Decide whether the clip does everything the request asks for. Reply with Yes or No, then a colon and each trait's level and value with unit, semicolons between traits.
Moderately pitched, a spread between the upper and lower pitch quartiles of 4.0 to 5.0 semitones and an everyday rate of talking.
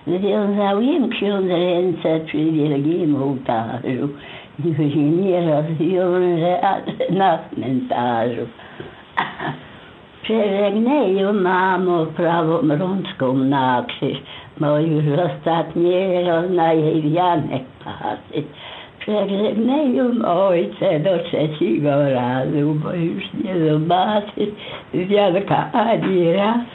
No: medium, 170 Hz; average, 4.3 semitones; slow, 85 wpm